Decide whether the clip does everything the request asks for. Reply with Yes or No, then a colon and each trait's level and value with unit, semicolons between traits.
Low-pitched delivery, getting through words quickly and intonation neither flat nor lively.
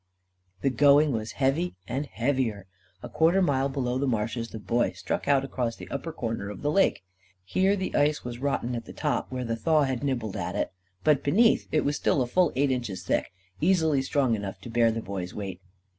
Yes: low, 130 Hz; fast, 210 wpm; average, 4.1 semitones